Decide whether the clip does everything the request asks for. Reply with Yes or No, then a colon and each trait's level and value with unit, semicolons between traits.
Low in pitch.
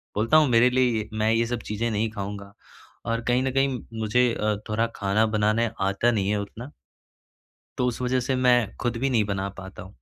Yes: low, 115 Hz